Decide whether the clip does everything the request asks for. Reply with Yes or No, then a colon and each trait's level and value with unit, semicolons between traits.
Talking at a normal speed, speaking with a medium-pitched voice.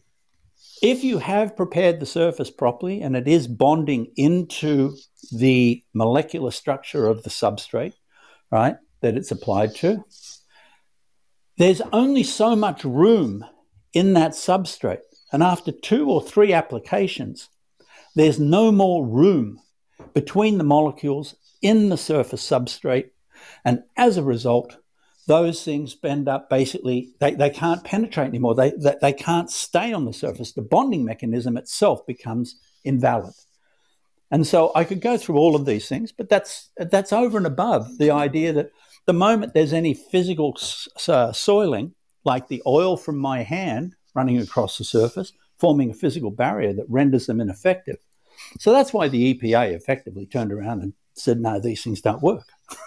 Yes: average, 150 wpm; medium, 150 Hz